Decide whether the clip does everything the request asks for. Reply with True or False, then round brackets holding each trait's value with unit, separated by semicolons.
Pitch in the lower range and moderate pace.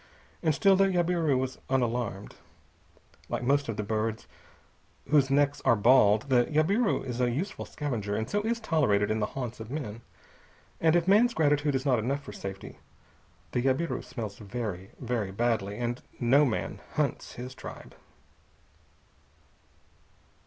True (125 Hz; 150 wpm)